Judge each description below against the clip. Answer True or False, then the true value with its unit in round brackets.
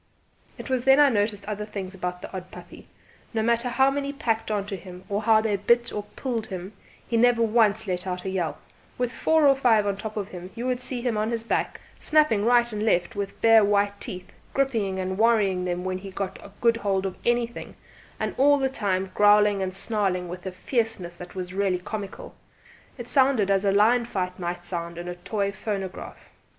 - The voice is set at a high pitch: True (205 Hz)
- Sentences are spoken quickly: True (215 wpm)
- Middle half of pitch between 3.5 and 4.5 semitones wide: True (3.8 semitones)